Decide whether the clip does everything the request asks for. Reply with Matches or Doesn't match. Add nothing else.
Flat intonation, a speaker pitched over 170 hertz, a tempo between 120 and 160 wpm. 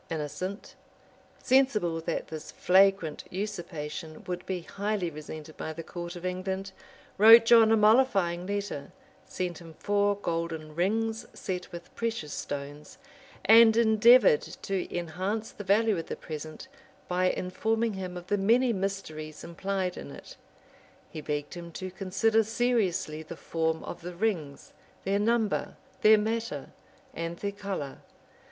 Doesn't match